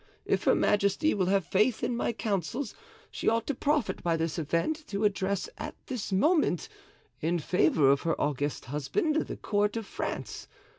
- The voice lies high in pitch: Yes, high, 200 Hz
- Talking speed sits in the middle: Yes, average, 170 wpm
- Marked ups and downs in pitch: Yes, wide, 6.1 semitones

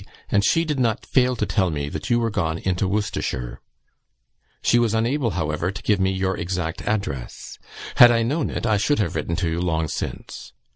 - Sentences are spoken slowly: No, average, 200 wpm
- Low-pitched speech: Yes, low, 100 Hz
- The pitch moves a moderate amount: No, wide, 5.7 semitones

